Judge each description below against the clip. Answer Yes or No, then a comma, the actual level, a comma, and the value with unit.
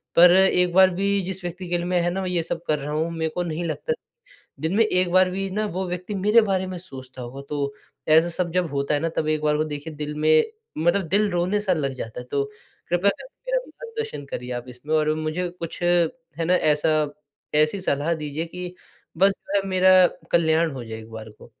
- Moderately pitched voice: Yes, medium, 170 Hz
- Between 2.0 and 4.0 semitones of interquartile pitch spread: Yes, average, 3.5 semitones